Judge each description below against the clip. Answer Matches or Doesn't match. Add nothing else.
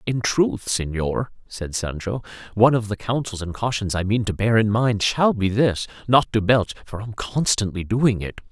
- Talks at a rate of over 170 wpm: Matches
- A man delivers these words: Matches